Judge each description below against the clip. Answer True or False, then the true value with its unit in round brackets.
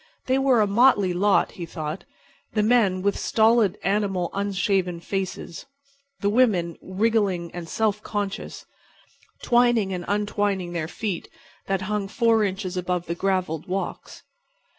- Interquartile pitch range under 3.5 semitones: True (2.9 semitones)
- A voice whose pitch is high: True (195 Hz)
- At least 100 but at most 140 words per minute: True (135 wpm)